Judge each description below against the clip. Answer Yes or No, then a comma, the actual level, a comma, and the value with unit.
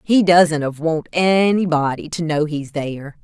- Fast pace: No, average, 165 wpm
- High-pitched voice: No, medium, 160 Hz